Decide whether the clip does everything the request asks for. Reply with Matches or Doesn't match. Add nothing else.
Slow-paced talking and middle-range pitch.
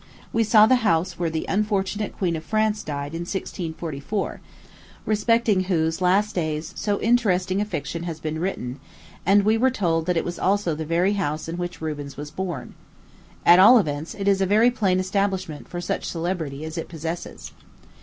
Doesn't match